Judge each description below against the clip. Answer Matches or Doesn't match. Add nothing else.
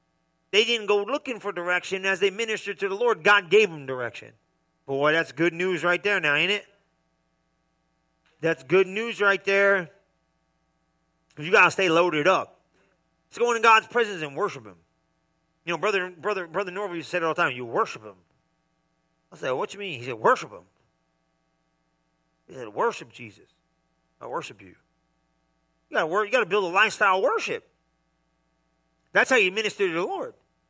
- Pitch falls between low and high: Matches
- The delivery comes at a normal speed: Matches